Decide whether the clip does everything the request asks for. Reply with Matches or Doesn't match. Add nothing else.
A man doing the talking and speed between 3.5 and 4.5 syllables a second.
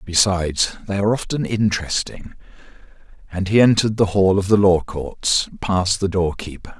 Doesn't match